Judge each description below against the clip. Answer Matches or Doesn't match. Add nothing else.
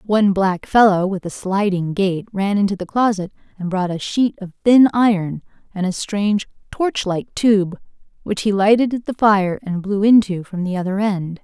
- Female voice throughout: Matches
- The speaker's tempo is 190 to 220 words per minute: Matches